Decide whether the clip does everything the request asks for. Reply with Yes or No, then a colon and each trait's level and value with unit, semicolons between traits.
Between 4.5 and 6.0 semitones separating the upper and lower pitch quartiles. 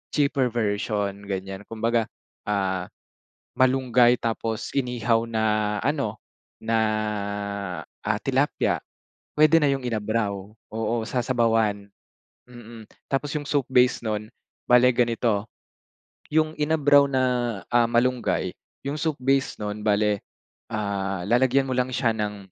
No: average, 3.6 semitones